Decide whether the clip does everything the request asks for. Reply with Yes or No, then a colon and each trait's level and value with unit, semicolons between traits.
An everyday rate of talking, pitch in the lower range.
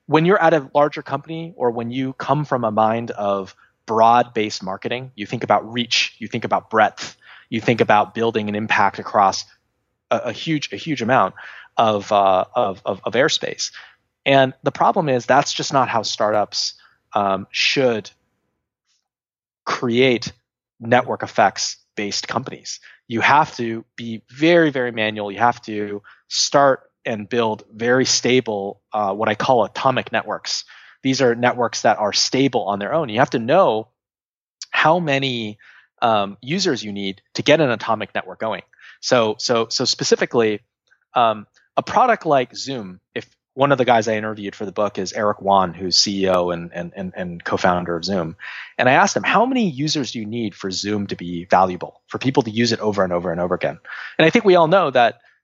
Yes: average, 185 wpm; low, 115 Hz